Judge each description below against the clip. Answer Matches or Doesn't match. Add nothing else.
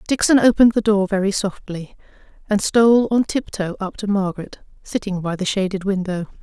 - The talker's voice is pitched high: Matches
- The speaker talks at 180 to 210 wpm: Doesn't match